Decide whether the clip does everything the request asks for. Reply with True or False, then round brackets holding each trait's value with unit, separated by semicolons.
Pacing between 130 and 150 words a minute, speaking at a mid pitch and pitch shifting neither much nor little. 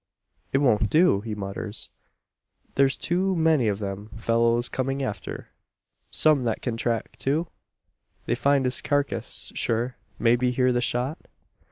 False (140 wpm; 125 Hz; 3.6 semitones)